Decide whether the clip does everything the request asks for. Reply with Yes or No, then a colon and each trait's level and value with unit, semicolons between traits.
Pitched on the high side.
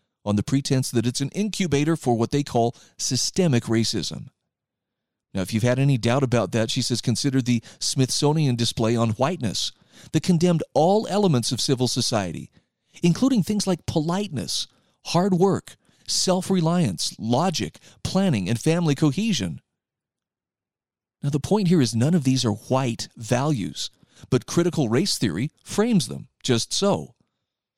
No: low, 135 Hz